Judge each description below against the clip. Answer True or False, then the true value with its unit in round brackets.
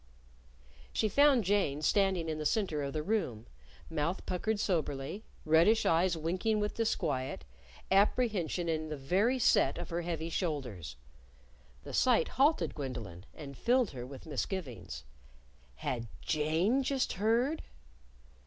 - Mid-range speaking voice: True (170 Hz)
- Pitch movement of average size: False (7.0 semitones)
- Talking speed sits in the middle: False (130 wpm)